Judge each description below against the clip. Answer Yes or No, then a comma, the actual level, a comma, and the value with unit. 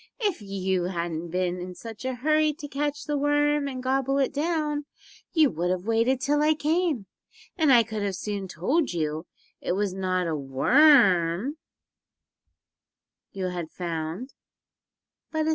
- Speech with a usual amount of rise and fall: No, wide, 8.3 semitones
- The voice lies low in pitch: No, high, 230 Hz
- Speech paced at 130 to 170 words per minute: Yes, average, 160 wpm